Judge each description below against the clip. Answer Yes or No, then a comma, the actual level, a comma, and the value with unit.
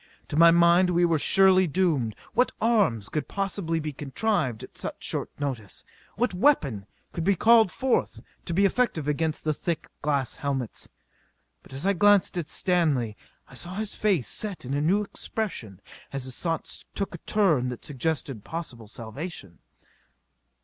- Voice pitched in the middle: Yes, medium, 165 Hz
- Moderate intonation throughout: No, wide, 6.3 semitones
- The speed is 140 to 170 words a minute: Yes, average, 165 wpm